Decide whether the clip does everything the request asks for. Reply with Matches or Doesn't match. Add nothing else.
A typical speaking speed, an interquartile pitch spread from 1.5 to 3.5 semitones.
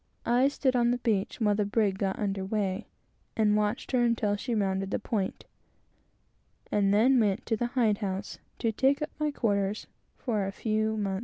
Matches